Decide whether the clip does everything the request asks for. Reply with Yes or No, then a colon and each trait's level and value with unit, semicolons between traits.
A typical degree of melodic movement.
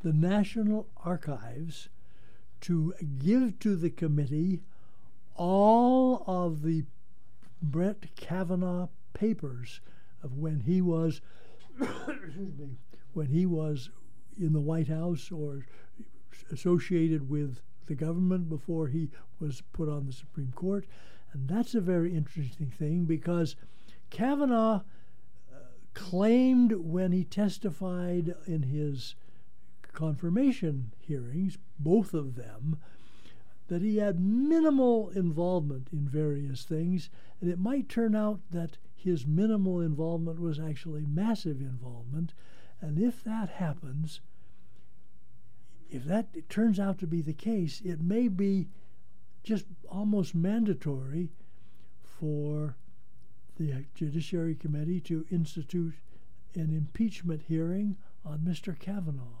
Yes: average, 4.2 semitones